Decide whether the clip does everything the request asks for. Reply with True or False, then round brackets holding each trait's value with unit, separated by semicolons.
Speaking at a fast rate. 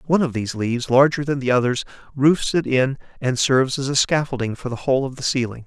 True (235 wpm)